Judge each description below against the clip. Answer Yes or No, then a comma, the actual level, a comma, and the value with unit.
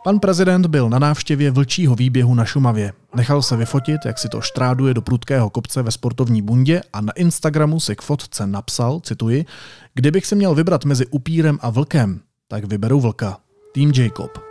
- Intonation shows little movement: No, average, 4.2 semitones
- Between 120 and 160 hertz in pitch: Yes, low, 135 Hz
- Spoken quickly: Yes, fast, 180 wpm